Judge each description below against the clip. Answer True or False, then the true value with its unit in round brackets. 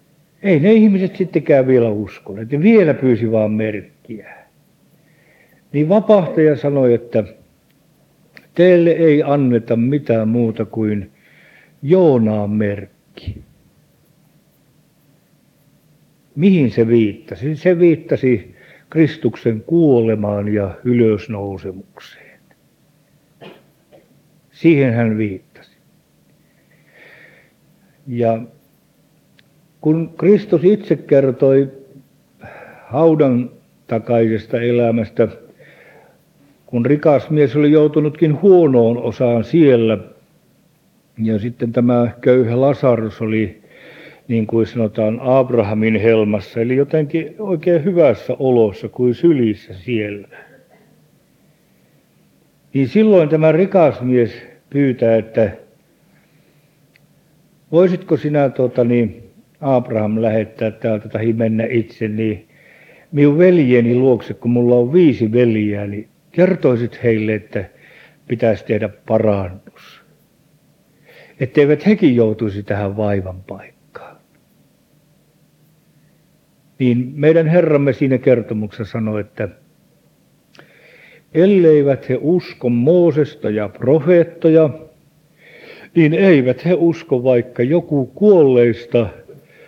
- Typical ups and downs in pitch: False (5.8 semitones)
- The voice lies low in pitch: True (130 Hz)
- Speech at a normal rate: False (85 wpm)